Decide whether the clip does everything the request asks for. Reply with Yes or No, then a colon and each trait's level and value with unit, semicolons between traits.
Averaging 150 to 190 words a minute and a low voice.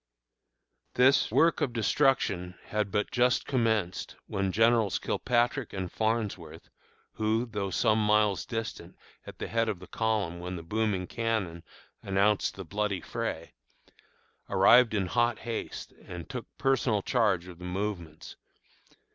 No: slow, 135 wpm; low, 105 Hz